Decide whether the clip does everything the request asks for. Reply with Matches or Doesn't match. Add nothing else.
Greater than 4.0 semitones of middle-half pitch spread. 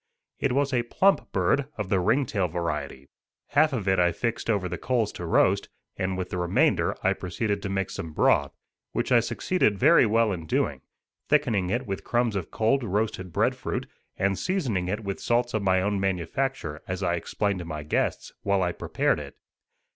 Matches